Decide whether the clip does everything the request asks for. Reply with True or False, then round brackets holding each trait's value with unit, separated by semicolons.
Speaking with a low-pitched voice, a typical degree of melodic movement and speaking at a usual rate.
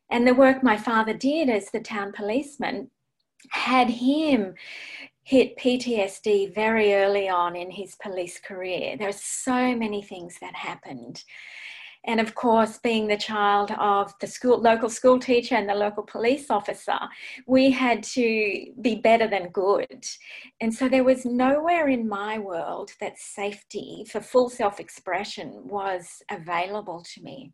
False (220 Hz; 3.8 semitones; 155 wpm)